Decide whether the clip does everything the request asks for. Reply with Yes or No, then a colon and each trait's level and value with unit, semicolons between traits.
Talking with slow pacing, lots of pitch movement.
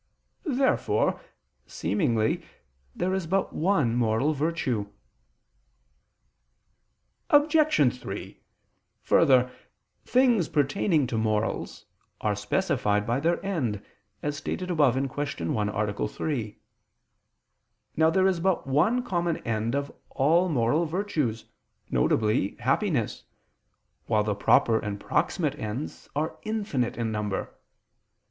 Yes: slow, 105 wpm; wide, 7.7 semitones